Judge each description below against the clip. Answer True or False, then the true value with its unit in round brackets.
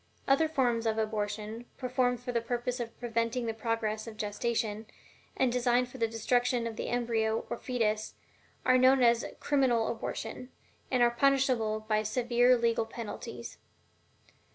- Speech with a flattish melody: True (2.0 semitones)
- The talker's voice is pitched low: False (235 Hz)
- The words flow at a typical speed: True (155 wpm)